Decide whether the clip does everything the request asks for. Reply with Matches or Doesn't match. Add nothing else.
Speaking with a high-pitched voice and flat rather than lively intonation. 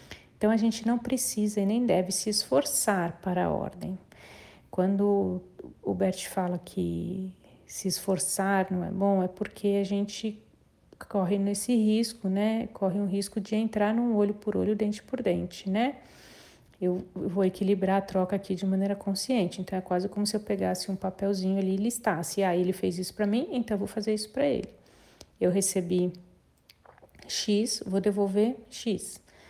Matches